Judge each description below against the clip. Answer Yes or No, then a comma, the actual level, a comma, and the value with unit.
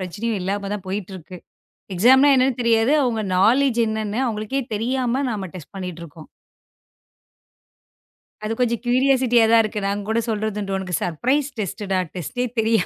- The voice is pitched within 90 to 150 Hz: No, high, 220 Hz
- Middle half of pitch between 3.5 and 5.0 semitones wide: Yes, average, 4.0 semitones